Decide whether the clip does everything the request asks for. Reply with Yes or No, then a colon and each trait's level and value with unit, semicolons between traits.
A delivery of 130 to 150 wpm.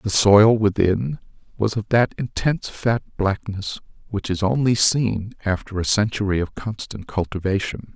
Yes: average, 145 wpm